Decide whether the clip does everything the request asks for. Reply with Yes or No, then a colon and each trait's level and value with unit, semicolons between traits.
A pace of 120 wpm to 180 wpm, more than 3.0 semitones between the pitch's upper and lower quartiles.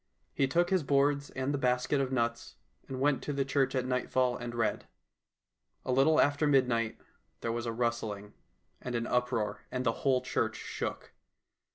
No: average, 175 wpm; average, 2.7 semitones